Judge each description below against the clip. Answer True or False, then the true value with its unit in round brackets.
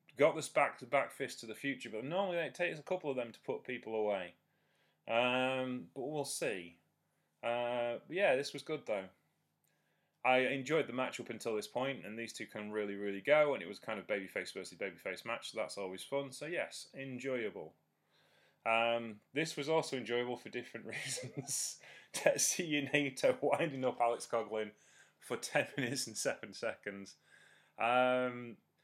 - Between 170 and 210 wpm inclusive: True (175 wpm)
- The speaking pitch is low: True (125 Hz)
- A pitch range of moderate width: True (4.1 semitones)